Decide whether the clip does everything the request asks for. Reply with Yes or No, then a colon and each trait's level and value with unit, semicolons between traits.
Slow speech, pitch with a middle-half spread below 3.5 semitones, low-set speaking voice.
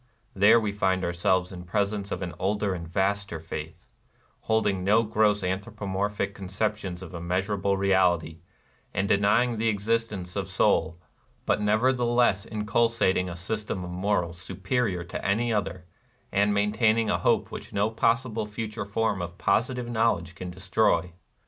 No: average, 155 wpm; average, 3.0 semitones; low, 100 Hz